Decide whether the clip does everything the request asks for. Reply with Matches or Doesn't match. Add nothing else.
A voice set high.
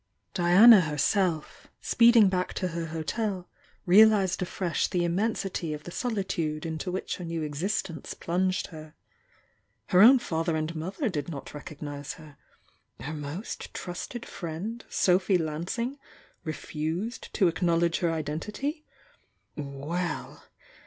Doesn't match